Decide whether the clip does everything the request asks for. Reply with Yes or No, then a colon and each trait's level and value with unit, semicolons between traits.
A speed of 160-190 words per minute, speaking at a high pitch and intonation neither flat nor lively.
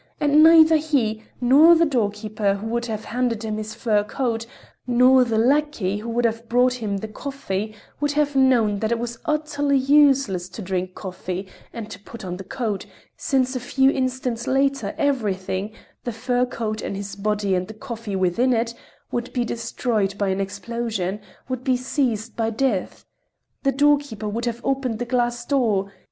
Yes: average, 170 wpm; high, 235 Hz; average, 4.0 semitones